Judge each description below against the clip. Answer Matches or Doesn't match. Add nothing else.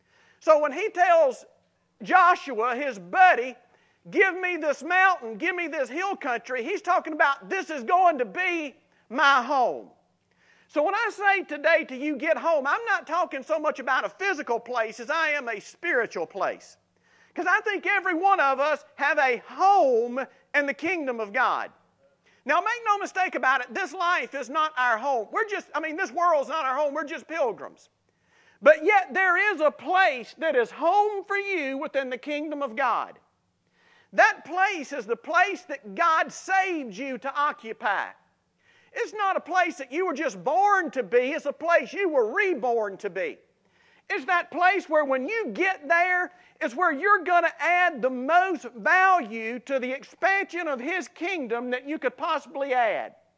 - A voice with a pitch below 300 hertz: Doesn't match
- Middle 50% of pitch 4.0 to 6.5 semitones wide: Matches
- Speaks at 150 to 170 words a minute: Doesn't match